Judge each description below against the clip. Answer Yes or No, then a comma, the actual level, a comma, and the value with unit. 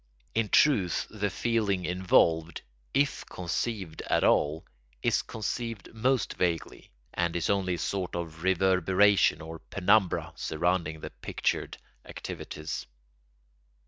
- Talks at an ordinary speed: No, slow, 110 wpm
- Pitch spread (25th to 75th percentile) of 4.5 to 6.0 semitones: No, average, 3.7 semitones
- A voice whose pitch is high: No, very low, 95 Hz